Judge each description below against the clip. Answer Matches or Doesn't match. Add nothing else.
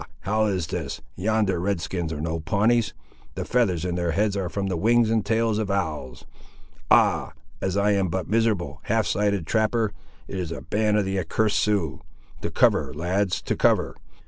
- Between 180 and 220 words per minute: Matches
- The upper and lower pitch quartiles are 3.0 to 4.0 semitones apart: Matches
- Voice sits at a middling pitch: Doesn't match